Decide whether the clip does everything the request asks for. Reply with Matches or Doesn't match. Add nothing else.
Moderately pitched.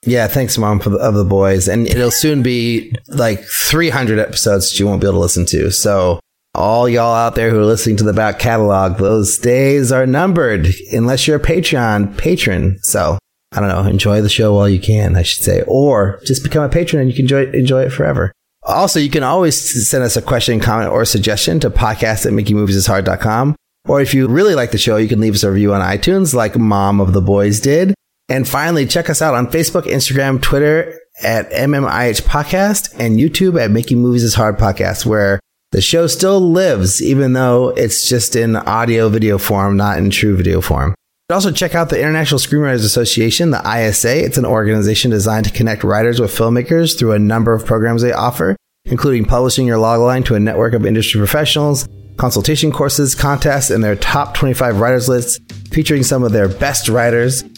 Doesn't match